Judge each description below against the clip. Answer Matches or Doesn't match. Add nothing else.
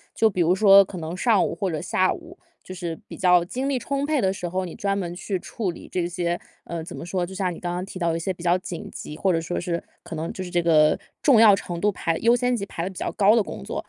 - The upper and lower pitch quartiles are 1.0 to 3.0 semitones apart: Matches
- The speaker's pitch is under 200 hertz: Matches